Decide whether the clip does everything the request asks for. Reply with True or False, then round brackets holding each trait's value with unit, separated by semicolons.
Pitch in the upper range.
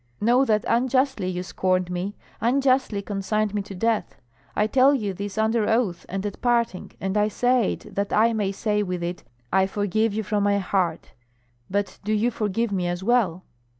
True (210 Hz)